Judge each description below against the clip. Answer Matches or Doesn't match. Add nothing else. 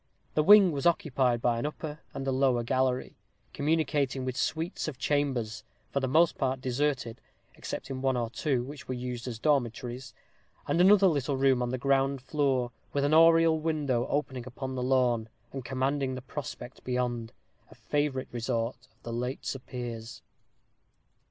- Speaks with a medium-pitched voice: Doesn't match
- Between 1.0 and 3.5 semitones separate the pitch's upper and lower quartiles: Matches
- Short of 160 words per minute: Doesn't match